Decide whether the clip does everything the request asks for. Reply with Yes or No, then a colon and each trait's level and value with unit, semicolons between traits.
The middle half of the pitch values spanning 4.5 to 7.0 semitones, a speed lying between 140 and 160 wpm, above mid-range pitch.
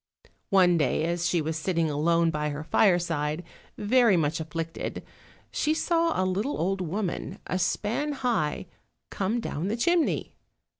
No: average, 5.1 semitones; average, 145 wpm; medium, 175 Hz